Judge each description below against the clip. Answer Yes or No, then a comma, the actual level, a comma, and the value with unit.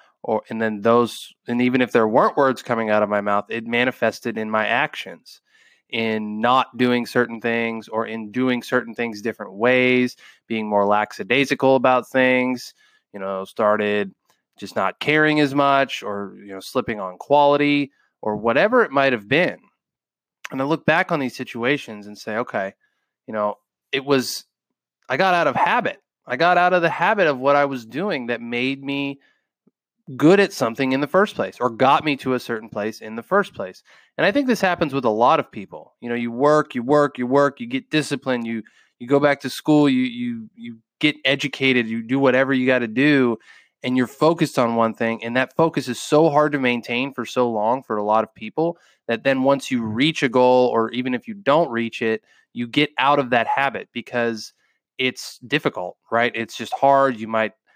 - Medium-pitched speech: No, low, 125 Hz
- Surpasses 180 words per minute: Yes, fast, 205 wpm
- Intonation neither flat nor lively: Yes, average, 3.9 semitones